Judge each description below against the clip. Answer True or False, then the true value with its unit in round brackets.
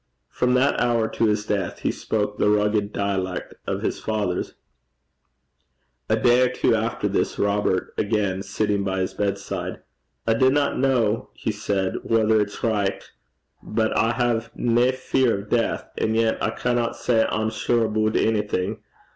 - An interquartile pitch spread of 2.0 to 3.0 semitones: True (2.4 semitones)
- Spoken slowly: False (155 wpm)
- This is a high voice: False (110 Hz)